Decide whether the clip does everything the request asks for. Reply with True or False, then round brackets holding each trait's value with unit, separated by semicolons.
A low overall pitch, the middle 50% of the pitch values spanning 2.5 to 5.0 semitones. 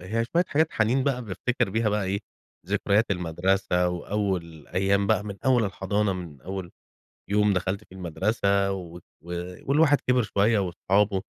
True (100 Hz; 2.8 semitones)